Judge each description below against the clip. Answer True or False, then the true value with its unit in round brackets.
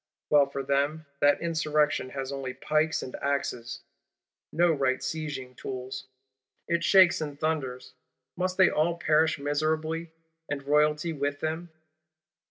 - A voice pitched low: False (150 Hz)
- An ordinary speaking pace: False (130 wpm)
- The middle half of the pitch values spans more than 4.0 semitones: False (2.4 semitones)